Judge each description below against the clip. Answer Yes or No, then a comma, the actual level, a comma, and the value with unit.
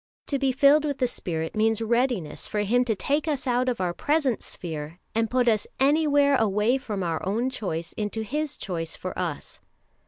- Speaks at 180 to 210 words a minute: Yes, average, 190 wpm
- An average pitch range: No, wide, 6.2 semitones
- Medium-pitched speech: No, high, 230 Hz